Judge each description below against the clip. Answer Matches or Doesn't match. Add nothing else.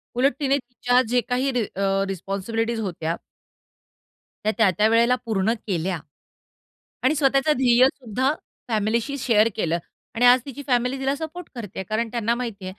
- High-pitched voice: Matches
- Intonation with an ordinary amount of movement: Matches